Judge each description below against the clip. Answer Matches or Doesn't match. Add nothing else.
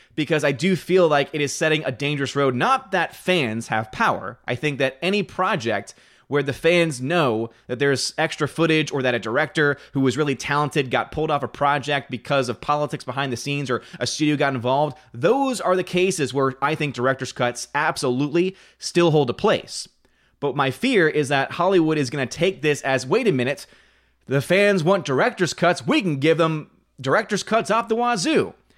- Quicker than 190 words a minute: Matches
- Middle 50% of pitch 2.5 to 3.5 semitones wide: Doesn't match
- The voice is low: Doesn't match